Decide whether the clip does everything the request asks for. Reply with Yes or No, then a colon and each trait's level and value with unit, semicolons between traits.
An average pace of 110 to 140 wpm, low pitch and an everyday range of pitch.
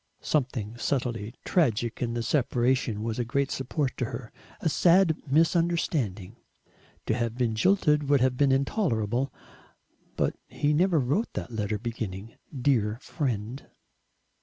Yes: slow, 135 wpm; low, 125 Hz; average, 4.4 semitones